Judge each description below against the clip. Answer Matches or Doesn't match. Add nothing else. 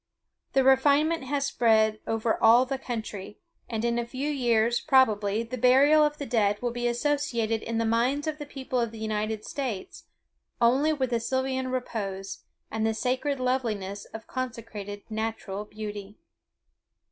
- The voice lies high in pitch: Matches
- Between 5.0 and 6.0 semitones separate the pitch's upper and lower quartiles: Doesn't match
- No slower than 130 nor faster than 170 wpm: Matches